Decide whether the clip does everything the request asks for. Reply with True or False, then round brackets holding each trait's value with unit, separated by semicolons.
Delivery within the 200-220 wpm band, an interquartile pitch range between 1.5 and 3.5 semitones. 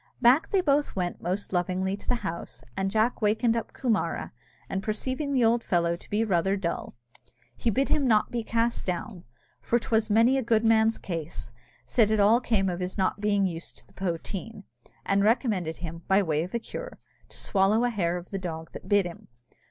False (205 wpm; 4.2 semitones)